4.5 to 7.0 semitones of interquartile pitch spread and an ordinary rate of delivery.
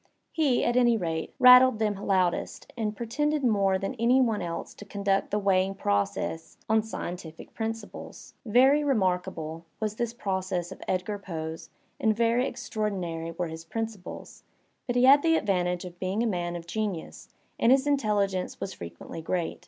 Yes: average, 4.8 semitones; average, 160 wpm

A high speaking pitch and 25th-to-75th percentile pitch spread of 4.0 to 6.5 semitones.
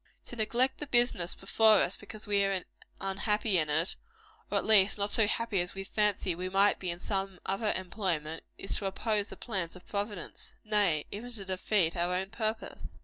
No: high, 195 Hz; average, 2.8 semitones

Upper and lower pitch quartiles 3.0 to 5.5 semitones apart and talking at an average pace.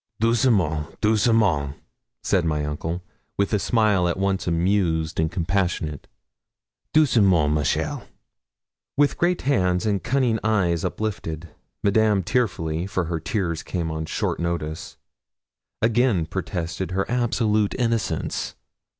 No: average, 5.0 semitones; slow, 115 wpm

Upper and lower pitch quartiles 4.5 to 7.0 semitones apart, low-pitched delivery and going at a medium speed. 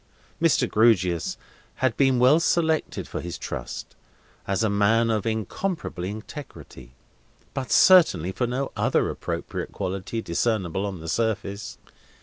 No: average, 5.2 semitones; low, 110 Hz; slow, 130 wpm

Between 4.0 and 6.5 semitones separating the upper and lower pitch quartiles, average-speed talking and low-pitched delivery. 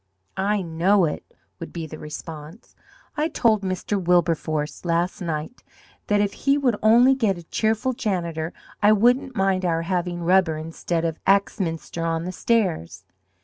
No: average, 4.3 semitones; average, 150 wpm; medium, 180 Hz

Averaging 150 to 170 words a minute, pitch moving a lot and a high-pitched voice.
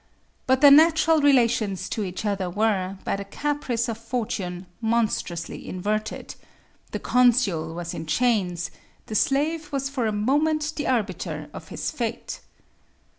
No: average, 140 wpm; wide, 6.0 semitones; high, 225 Hz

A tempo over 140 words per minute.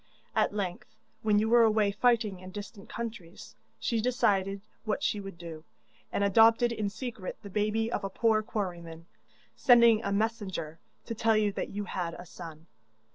Yes: average, 170 wpm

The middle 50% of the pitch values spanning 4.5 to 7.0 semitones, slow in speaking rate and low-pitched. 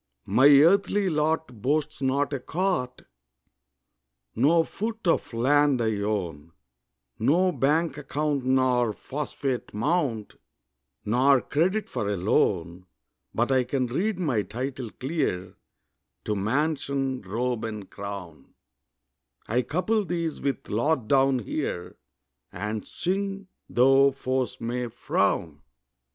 Yes: wide, 5.6 semitones; slow, 110 wpm; low, 130 Hz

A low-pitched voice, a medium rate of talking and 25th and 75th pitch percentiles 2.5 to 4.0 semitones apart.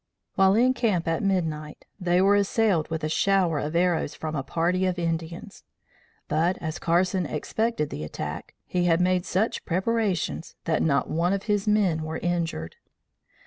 No: medium, 175 Hz; average, 165 wpm; average, 3.3 semitones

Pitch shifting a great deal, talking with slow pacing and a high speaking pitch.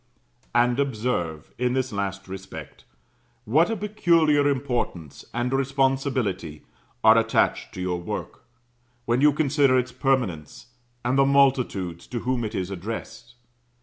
No: wide, 5.9 semitones; slow, 130 wpm; low, 125 Hz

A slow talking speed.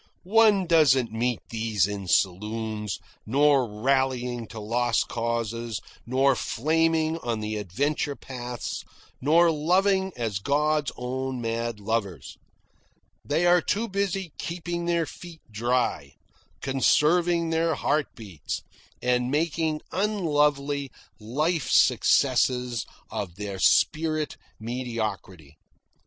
Yes: slow, 105 wpm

